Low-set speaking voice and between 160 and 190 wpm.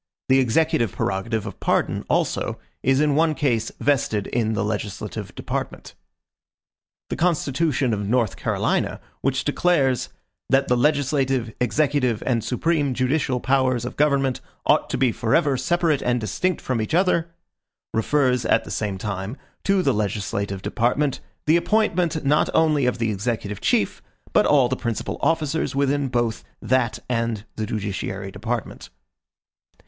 No: low, 130 Hz; average, 145 wpm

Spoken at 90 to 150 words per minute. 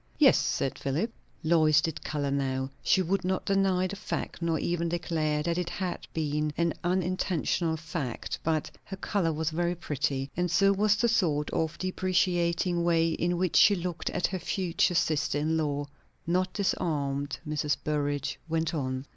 No: average, 165 wpm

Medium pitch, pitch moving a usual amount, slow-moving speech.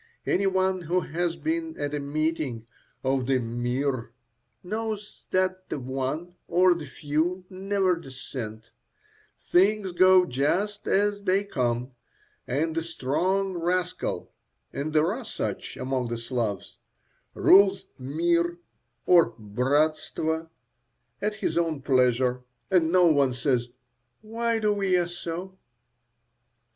No: medium, 165 Hz; wide, 6.0 semitones; slow, 120 wpm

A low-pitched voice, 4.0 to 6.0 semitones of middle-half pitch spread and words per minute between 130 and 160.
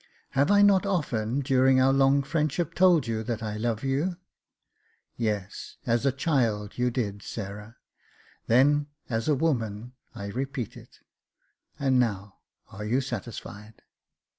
Yes: low, 125 Hz; average, 4.4 semitones; average, 150 wpm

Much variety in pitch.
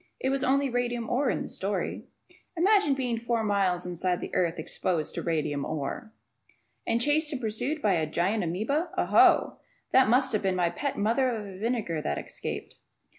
Yes: wide, 6.4 semitones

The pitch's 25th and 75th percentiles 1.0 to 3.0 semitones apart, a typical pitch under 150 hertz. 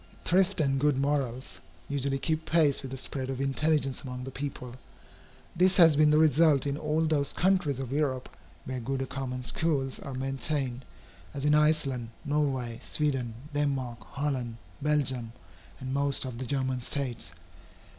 Yes: narrow, 2.6 semitones; low, 135 Hz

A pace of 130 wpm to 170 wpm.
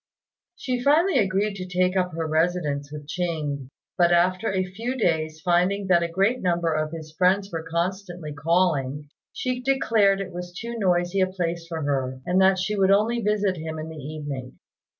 No: average, 185 wpm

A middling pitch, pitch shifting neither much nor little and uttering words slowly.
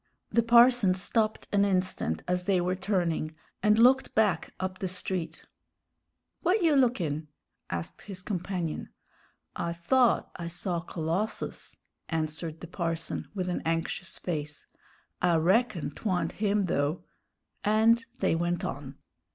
Yes: medium, 180 Hz; average, 4.3 semitones; slow, 130 wpm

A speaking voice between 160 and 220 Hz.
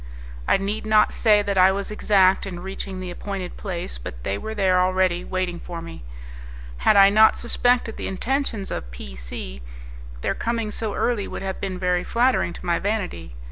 Yes: high, 190 Hz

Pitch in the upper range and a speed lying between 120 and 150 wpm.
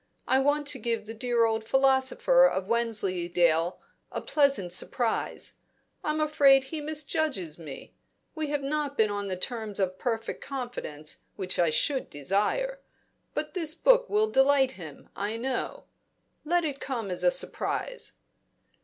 Yes: very high, 250 Hz; average, 145 wpm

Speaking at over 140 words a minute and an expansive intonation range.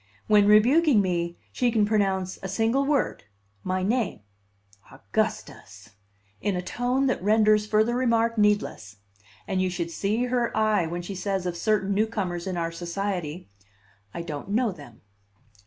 No: average, 150 wpm; average, 3.9 semitones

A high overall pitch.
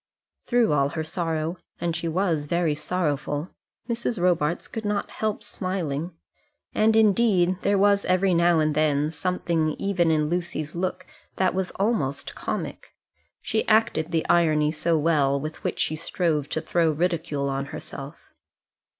No: medium, 170 Hz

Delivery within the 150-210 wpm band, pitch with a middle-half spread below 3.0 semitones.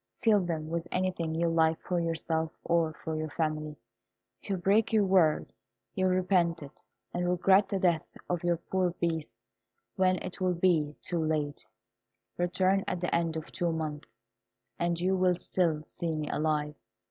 Yes: average, 170 wpm; narrow, 2.4 semitones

